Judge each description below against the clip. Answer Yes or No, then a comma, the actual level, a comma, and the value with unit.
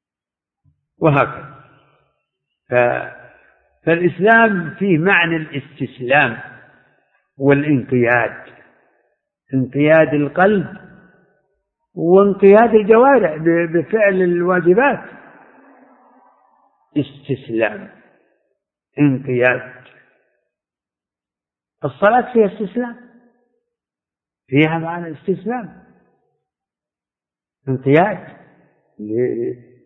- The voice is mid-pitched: Yes, medium, 170 Hz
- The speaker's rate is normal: No, slow, 40 wpm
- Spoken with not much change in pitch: No, wide, 7.1 semitones